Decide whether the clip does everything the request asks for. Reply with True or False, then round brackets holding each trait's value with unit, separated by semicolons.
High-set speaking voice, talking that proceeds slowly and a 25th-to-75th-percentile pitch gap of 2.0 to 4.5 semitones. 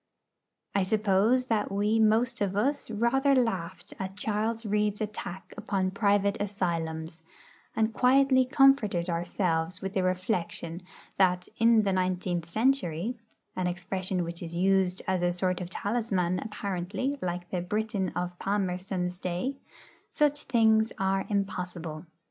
True (195 Hz; 130 wpm; 3.5 semitones)